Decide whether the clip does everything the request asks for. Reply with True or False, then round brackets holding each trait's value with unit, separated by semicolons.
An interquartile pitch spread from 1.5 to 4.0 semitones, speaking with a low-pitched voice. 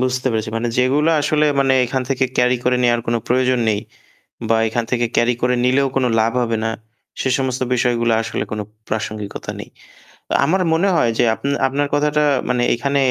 True (2.5 semitones; 125 Hz)